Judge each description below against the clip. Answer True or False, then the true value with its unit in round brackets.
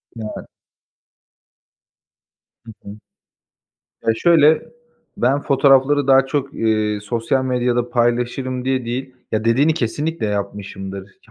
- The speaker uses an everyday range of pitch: True (3.3 semitones)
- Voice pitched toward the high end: False (125 Hz)